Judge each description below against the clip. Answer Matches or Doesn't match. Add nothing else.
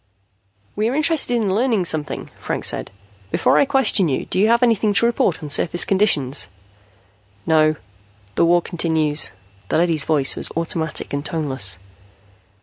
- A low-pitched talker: Doesn't match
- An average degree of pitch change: Doesn't match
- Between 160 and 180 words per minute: Doesn't match